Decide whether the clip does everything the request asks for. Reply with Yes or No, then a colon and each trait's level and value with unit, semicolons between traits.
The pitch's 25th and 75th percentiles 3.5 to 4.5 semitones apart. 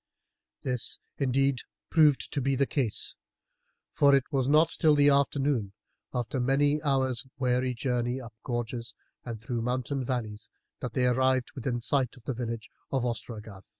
No: narrow, 2.5 semitones